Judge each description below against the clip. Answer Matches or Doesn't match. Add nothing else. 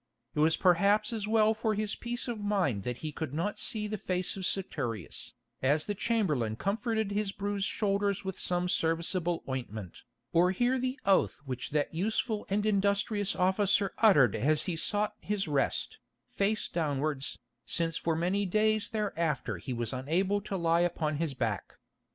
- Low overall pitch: Doesn't match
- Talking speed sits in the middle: Matches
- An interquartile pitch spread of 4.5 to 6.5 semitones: Matches